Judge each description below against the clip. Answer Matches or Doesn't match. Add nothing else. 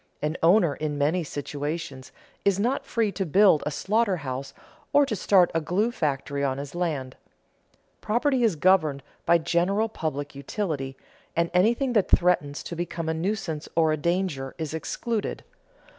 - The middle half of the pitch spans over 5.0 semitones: Matches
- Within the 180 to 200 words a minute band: Doesn't match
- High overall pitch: Doesn't match